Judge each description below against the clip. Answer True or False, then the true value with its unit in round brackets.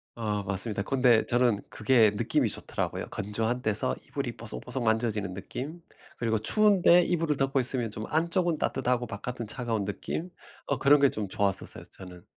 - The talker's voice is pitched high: False (115 Hz)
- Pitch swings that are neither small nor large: True (4.7 semitones)